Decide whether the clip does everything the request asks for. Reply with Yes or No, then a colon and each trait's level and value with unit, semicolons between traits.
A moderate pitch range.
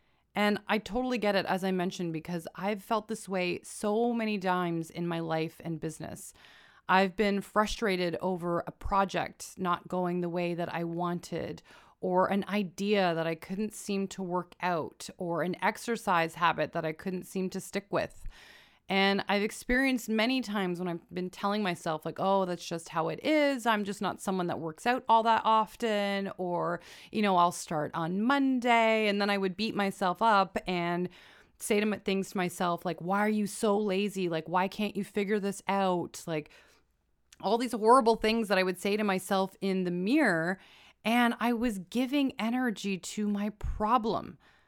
Yes: average, 3.3 semitones